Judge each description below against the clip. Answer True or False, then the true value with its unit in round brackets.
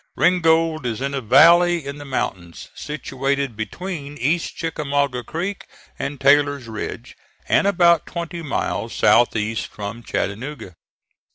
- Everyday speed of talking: False (125 wpm)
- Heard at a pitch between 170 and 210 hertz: False (140 Hz)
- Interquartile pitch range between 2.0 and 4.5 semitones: False (5.0 semitones)